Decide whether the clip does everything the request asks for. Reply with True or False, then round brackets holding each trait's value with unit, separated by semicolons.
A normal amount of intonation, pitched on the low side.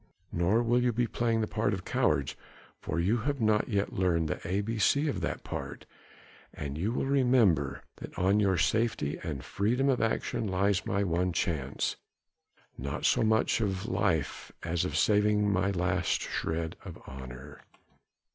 True (5.0 semitones; 100 Hz)